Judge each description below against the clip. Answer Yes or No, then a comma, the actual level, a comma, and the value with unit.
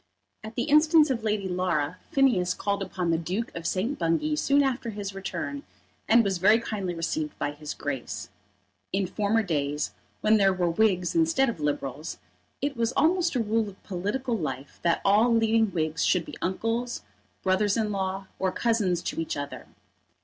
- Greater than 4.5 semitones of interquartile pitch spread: Yes, average, 4.9 semitones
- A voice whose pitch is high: Yes, high, 200 Hz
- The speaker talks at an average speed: Yes, average, 175 wpm